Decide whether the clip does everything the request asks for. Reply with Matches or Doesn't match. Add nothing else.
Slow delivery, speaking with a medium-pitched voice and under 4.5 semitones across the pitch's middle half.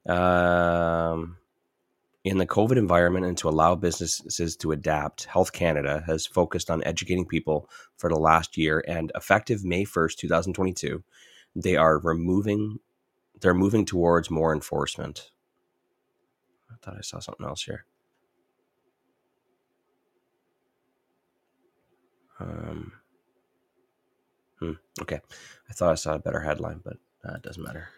Doesn't match